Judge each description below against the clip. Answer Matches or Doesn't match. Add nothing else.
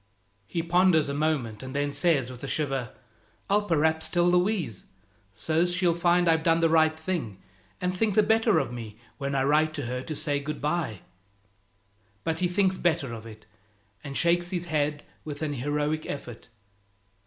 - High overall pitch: Doesn't match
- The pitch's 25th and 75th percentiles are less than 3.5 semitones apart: Doesn't match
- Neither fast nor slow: Matches